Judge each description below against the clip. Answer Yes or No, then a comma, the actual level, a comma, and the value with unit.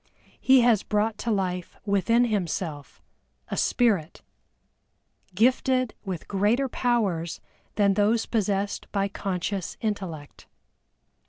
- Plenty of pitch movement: No, average, 3.8 semitones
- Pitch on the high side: Yes, high, 205 Hz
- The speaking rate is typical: No, slow, 100 wpm